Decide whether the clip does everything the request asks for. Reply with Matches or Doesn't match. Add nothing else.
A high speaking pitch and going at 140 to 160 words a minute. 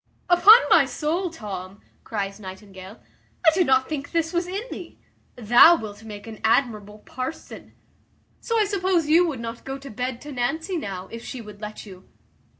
Doesn't match